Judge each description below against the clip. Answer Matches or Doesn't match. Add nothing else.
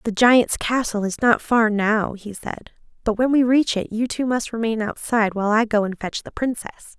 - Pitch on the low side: Doesn't match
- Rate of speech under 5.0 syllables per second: Doesn't match